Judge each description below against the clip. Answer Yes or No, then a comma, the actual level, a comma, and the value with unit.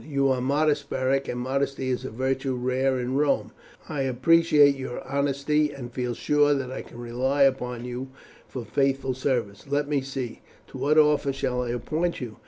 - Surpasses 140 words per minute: Yes, average, 190 wpm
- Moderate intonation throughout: No, narrow, 2.2 semitones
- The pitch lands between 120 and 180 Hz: Yes, low, 135 Hz